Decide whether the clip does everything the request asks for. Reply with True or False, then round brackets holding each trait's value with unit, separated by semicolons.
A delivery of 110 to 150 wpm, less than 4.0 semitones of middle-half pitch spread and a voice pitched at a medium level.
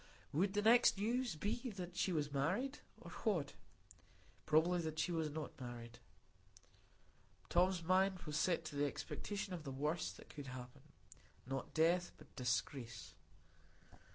False (135 wpm; 5.0 semitones; 165 Hz)